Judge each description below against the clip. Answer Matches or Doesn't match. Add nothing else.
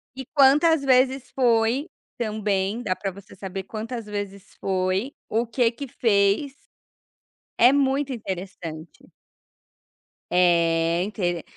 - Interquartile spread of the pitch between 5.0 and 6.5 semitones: Matches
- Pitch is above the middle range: Matches